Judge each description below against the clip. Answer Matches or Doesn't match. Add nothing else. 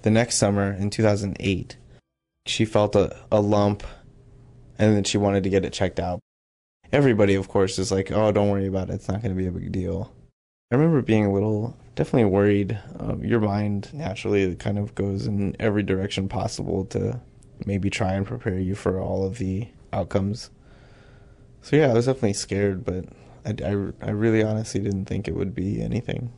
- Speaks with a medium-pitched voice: Doesn't match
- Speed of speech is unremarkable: Matches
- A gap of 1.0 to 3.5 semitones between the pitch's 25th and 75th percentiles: Matches